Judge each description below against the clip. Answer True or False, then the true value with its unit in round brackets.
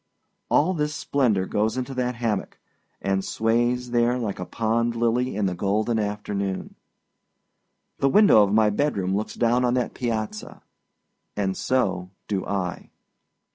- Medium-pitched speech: False (110 Hz)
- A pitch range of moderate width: True (3.7 semitones)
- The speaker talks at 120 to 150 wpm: True (140 wpm)